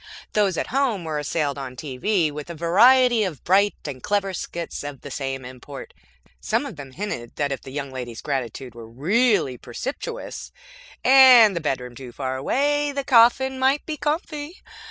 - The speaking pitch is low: No, medium, 170 Hz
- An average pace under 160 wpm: No, average, 175 wpm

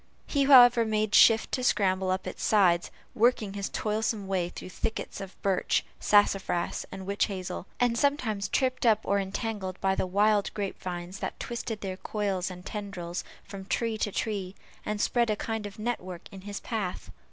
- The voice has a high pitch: Yes, high, 200 Hz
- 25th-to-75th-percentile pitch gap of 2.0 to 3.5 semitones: Yes, average, 2.8 semitones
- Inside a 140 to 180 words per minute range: Yes, average, 175 wpm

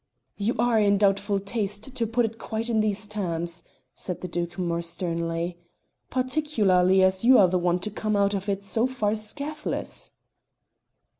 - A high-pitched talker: Yes, high, 200 Hz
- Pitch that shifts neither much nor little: Yes, average, 3.7 semitones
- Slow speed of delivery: No, average, 165 wpm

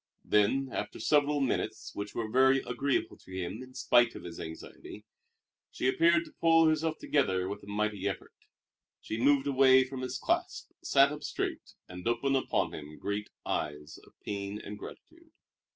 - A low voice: Yes, low, 125 Hz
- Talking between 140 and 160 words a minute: No, average, 170 wpm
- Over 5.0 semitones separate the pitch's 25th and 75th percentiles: Yes, wide, 5.4 semitones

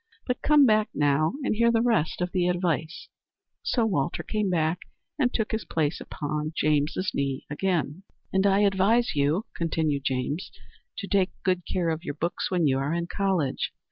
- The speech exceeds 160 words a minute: Yes, average, 175 wpm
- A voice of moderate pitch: Yes, medium, 175 Hz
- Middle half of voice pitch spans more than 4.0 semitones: Yes, average, 4.9 semitones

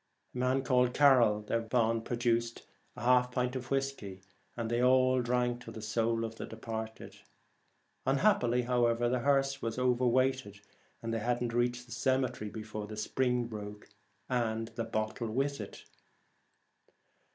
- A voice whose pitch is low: Yes, low, 120 Hz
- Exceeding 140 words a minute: Yes, average, 155 wpm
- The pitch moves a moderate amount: No, narrow, 2.0 semitones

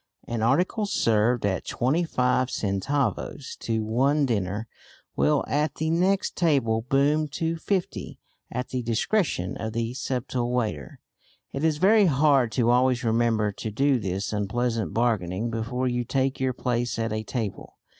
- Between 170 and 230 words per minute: No, average, 150 wpm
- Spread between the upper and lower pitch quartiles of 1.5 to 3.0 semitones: No, average, 4.1 semitones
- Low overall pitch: Yes, low, 125 Hz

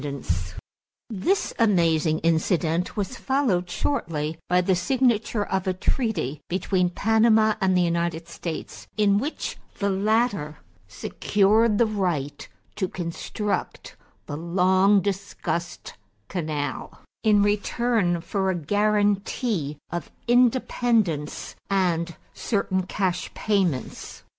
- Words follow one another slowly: Yes, slow, 110 wpm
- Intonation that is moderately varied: Yes, average, 4.1 semitones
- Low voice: No, high, 190 Hz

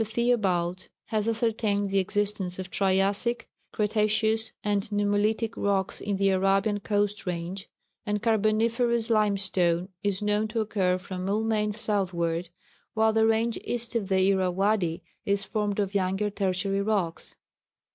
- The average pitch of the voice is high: Yes, high, 205 Hz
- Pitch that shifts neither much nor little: No, narrow, 2.3 semitones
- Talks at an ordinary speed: No, slow, 130 wpm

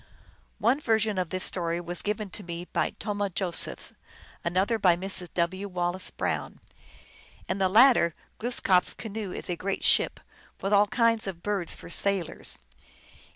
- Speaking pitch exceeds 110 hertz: Yes, high, 190 Hz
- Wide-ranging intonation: No, average, 2.9 semitones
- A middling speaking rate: Yes, average, 155 wpm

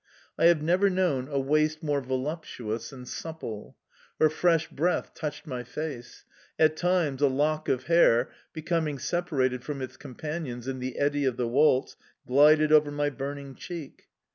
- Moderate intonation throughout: Yes, average, 3.2 semitones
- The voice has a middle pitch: Yes, medium, 145 Hz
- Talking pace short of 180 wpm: Yes, average, 160 wpm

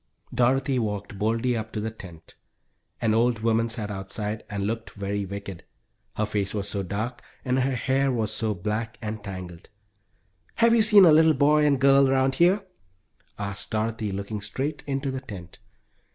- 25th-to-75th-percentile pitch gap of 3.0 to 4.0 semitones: No, average, 4.6 semitones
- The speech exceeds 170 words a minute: No, average, 165 wpm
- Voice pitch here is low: Yes, low, 110 Hz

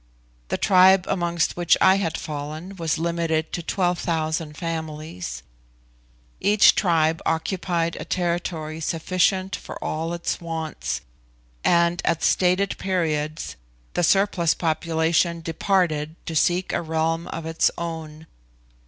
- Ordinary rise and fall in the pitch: No, narrow, 1.8 semitones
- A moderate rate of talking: No, slow, 120 wpm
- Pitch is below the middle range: No, medium, 165 Hz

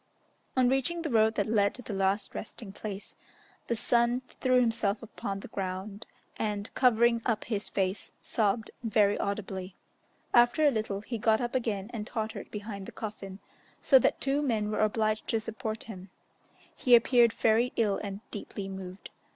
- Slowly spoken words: No, average, 165 wpm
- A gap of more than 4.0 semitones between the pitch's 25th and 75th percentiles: No, average, 2.9 semitones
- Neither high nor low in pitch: No, high, 220 Hz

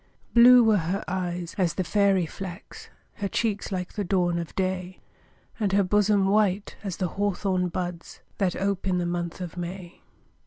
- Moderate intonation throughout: No, narrow, 2.2 semitones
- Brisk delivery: No, average, 170 wpm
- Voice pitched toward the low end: No, medium, 185 Hz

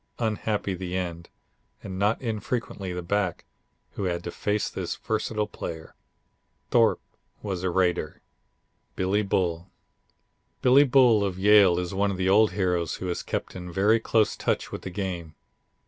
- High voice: No, very low, 95 Hz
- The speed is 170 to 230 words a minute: No, average, 155 wpm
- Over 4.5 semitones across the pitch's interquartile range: No, average, 3.0 semitones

